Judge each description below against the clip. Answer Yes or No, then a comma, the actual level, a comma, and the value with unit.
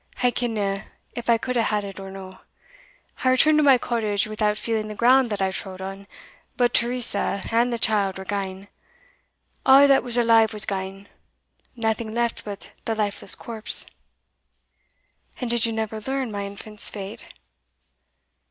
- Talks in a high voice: Yes, high, 220 Hz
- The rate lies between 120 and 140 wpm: No, average, 160 wpm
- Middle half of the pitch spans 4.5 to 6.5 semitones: No, average, 3.1 semitones